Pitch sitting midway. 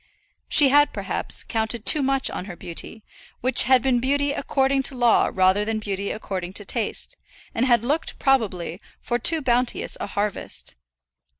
No: high, 240 Hz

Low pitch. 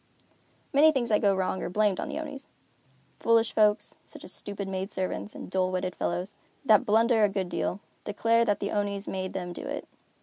No: high, 205 Hz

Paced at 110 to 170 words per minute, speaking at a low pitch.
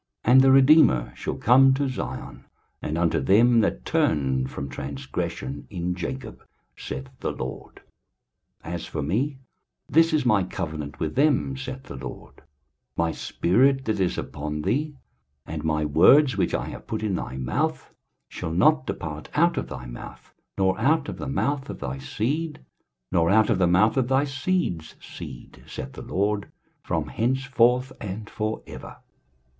Yes: average, 165 wpm; low, 105 Hz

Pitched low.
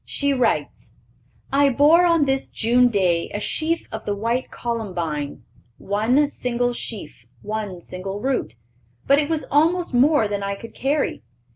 No: high, 240 Hz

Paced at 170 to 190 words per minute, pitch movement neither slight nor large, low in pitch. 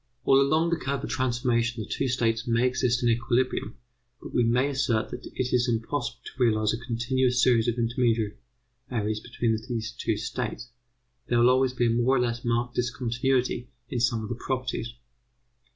No: average, 180 wpm; narrow, 1.6 semitones; low, 120 Hz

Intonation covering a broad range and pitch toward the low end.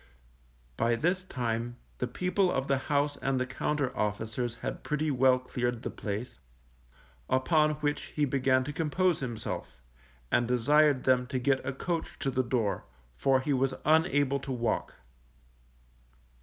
No: average, 3.2 semitones; low, 130 Hz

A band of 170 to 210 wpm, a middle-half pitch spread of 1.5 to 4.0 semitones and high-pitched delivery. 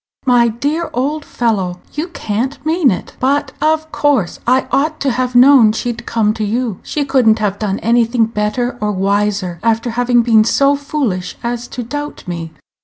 No: average, 180 wpm; average, 4.4 semitones; high, 240 Hz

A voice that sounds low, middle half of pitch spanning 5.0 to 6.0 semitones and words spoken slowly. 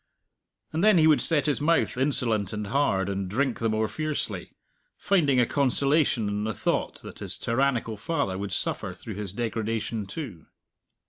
No: low, 115 Hz; wide, 5.6 semitones; average, 170 wpm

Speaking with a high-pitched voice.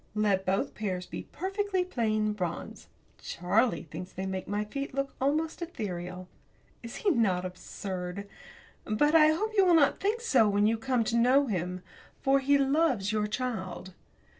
Yes: high, 220 Hz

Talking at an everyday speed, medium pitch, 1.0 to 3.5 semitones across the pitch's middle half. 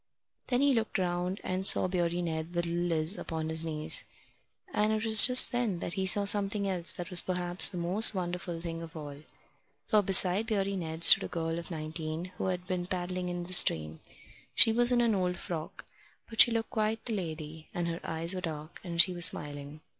No: fast, 210 wpm; medium, 180 Hz; average, 3.1 semitones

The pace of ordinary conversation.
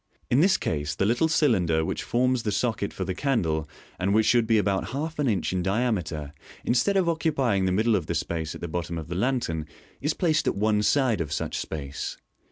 No: fast, 215 wpm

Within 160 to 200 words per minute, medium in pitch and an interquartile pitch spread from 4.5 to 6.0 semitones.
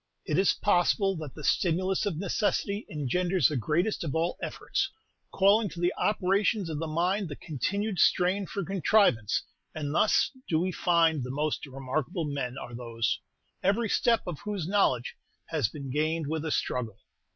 Yes: average, 165 wpm; medium, 165 Hz; average, 4.9 semitones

